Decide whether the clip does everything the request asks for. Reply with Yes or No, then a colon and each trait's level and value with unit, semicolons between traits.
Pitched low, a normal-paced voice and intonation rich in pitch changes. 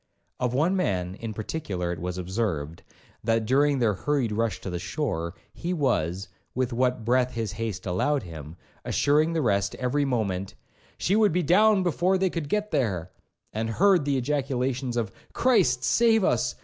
Yes: low, 125 Hz; average, 170 wpm; wide, 7.1 semitones